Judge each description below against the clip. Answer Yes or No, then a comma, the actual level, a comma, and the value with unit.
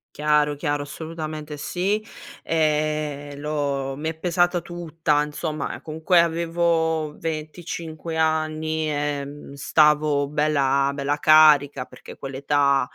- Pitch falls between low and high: Yes, medium, 155 Hz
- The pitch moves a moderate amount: No, narrow, 1.8 semitones